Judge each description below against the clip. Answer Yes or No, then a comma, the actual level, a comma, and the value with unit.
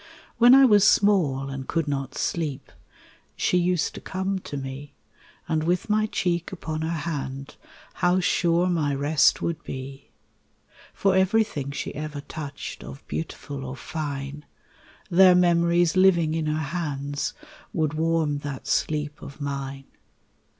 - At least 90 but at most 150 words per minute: Yes, average, 140 wpm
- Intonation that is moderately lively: Yes, average, 3.9 semitones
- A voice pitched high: No, medium, 155 Hz